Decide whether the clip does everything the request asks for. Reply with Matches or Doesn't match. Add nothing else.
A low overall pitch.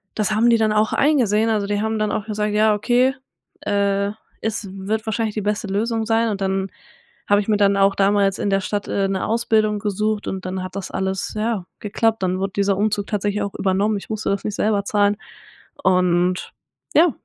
Doesn't match